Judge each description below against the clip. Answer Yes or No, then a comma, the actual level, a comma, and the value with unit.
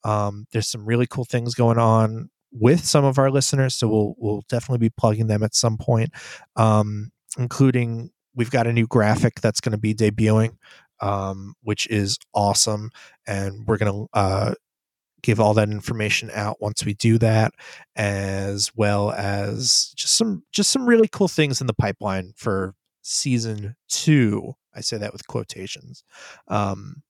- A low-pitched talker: Yes, low, 110 Hz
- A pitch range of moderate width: Yes, average, 3.0 semitones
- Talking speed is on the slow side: No, average, 165 wpm